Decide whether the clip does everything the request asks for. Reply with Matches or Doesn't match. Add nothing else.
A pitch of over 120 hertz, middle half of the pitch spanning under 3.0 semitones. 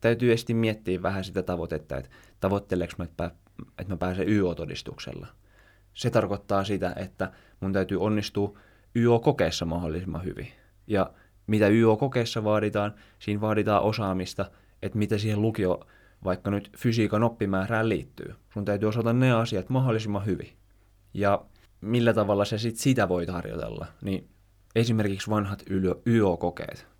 Doesn't match